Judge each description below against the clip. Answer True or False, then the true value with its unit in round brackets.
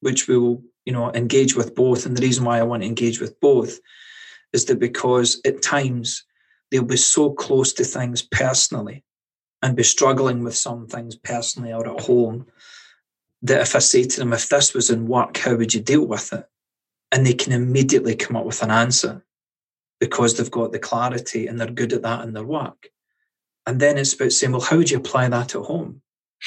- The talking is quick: True (210 wpm)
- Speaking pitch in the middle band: False (125 Hz)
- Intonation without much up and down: True (2.3 semitones)